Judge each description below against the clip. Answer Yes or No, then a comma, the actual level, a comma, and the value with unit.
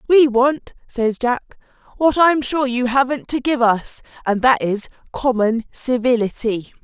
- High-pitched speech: Yes, very high, 250 Hz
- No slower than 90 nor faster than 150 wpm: Yes, average, 140 wpm